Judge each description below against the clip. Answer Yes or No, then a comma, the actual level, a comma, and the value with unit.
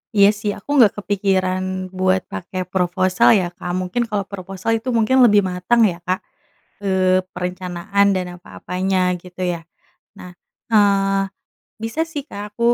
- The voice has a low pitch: No, high, 190 Hz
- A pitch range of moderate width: No, narrow, 1.9 semitones